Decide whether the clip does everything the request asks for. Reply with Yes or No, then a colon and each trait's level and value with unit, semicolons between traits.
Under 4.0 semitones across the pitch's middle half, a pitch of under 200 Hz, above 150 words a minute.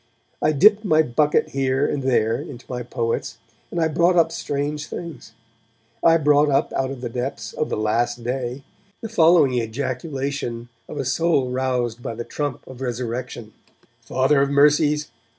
Yes: average, 3.6 semitones; low, 135 Hz; average, 165 wpm